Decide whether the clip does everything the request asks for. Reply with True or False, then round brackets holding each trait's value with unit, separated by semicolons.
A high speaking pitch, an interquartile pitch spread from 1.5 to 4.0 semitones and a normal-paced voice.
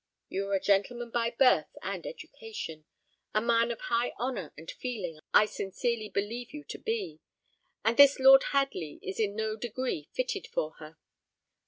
False (230 Hz; 4.8 semitones; 165 wpm)